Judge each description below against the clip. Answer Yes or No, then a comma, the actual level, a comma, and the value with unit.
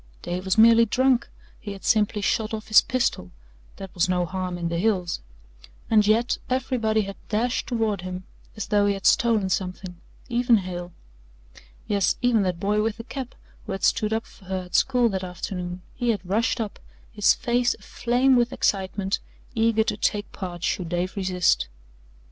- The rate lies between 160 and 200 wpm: Yes, average, 175 wpm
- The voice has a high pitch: Yes, high, 205 Hz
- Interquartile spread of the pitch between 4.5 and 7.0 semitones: No, average, 3.8 semitones